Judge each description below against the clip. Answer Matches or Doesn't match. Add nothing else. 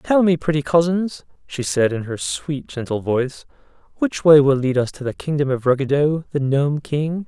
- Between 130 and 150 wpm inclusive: Doesn't match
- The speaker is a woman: Doesn't match